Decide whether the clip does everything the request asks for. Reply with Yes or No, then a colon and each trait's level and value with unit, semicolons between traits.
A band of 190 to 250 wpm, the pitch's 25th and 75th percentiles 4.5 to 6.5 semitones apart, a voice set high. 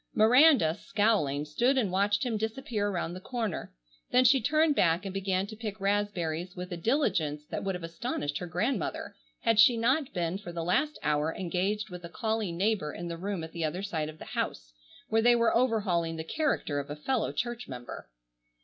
Yes: average, 200 wpm; wide, 5.4 semitones; high, 195 Hz